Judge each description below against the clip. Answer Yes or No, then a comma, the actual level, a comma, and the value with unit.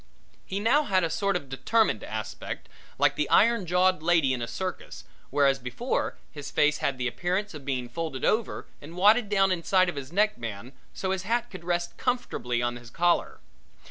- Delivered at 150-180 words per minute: No, average, 190 wpm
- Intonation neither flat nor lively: No, wide, 6.5 semitones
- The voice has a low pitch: No, medium, 175 Hz